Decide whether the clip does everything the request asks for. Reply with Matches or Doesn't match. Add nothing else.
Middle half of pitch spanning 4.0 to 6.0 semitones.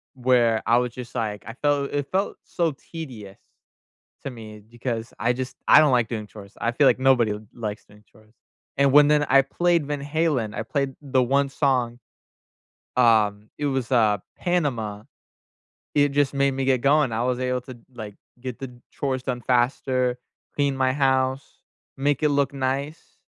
Doesn't match